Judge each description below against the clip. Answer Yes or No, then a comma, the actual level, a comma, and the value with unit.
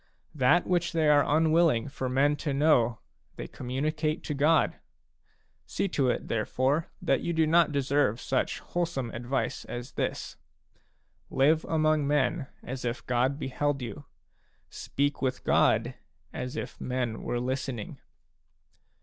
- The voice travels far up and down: No, average, 3.4 semitones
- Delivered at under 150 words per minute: Yes, average, 140 wpm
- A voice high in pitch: No, medium, 140 Hz